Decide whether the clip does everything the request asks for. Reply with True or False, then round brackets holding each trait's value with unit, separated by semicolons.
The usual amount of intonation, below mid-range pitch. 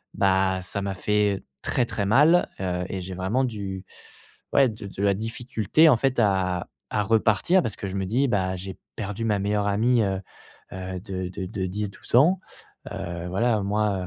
True (3.1 semitones; 100 Hz)